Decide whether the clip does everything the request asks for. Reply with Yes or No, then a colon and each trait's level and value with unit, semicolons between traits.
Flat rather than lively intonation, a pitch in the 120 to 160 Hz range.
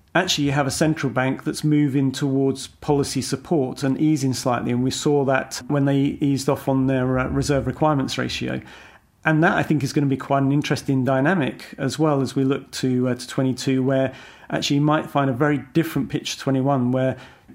Yes: narrow, 1.9 semitones; low, 135 Hz